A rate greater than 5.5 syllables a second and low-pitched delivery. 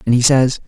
Yes: 6.0 syllables/s; low, 125 Hz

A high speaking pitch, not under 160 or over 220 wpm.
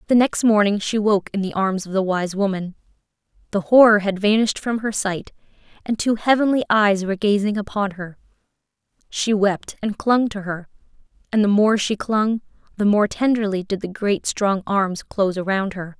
Yes: high, 205 Hz; average, 185 wpm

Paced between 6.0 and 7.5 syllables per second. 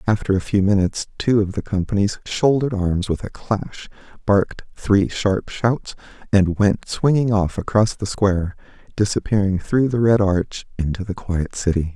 No: 4.7 syllables/s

